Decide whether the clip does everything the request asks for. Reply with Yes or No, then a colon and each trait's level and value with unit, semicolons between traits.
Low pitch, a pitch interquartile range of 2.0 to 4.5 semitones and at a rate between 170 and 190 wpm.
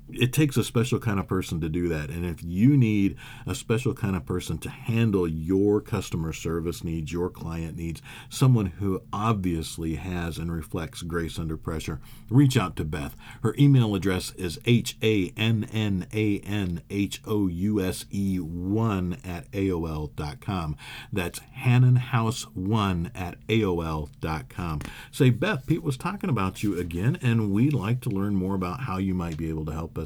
No: low, 100 Hz; average, 4.9 semitones; average, 175 wpm